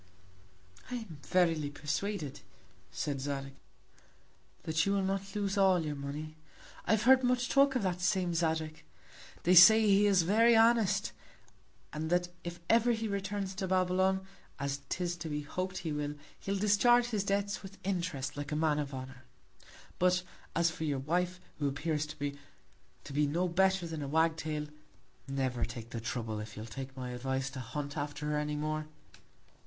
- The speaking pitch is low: No, medium, 165 Hz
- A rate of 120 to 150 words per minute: No, average, 175 wpm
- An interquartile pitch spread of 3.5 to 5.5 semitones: Yes, average, 5.1 semitones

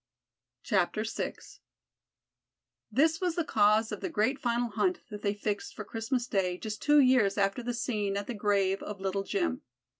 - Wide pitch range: No, average, 4.1 semitones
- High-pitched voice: Yes, high, 215 Hz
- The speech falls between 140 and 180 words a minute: Yes, average, 170 wpm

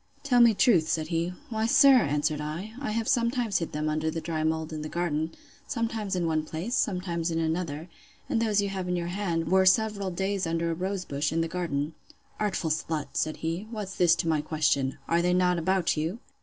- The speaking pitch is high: No, medium, 170 Hz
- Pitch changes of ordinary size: Yes, average, 4.0 semitones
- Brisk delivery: Yes, fast, 210 wpm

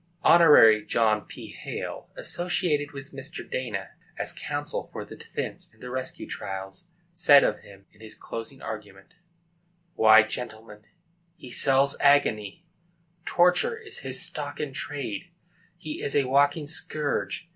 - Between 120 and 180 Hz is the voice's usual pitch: Yes, low, 135 Hz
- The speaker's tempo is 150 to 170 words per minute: No, average, 140 wpm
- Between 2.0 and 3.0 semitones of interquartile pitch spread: No, wide, 5.4 semitones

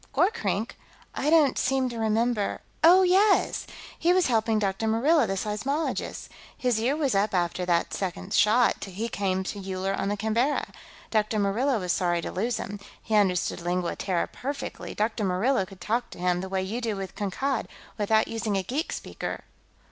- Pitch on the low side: No, high, 215 Hz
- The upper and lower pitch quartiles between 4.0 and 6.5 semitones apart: Yes, average, 4.6 semitones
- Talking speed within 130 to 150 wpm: No, average, 180 wpm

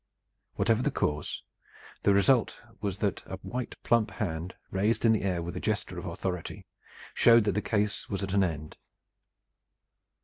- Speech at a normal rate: Yes, average, 165 wpm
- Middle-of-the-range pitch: No, low, 100 Hz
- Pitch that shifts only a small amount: No, average, 3.3 semitones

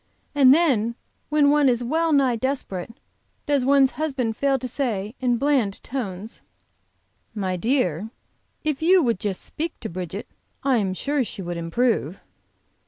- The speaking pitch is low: No, very high, 250 Hz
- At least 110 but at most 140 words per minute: No, average, 150 wpm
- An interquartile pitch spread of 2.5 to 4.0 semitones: No, wide, 5.5 semitones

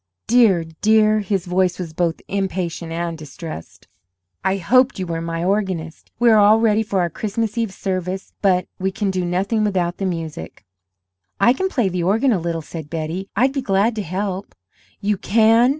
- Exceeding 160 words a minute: Yes, average, 180 wpm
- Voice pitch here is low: No, high, 190 Hz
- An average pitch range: Yes, average, 3.9 semitones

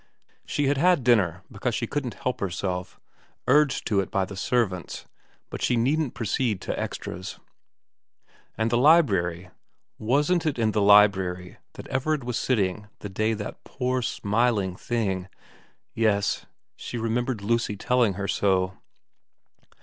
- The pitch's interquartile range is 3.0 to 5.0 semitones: Yes, average, 4.4 semitones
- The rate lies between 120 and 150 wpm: Yes, average, 140 wpm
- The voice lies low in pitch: Yes, low, 110 Hz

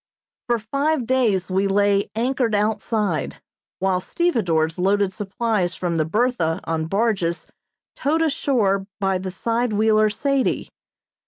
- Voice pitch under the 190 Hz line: No, high, 205 Hz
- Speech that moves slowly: Yes, slow, 120 wpm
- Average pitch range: Yes, average, 4.2 semitones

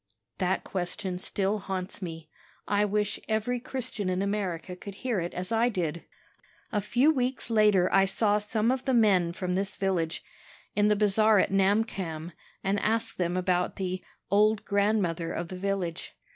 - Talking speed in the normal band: Yes, average, 165 wpm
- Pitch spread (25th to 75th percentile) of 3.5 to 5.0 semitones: No, average, 2.8 semitones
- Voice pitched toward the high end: Yes, high, 195 Hz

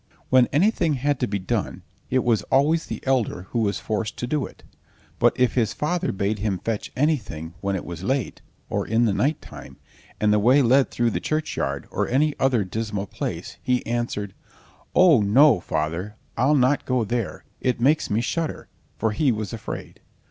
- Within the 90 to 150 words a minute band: No, average, 185 wpm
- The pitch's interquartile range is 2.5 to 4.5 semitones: No, average, 4.9 semitones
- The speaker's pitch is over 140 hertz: No, low, 120 Hz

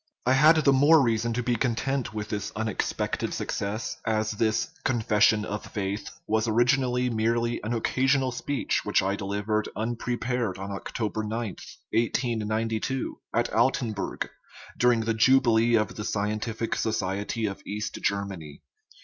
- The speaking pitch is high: No, low, 110 Hz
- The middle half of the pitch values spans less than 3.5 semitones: Yes, narrow, 2.4 semitones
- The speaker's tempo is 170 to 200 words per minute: No, average, 150 wpm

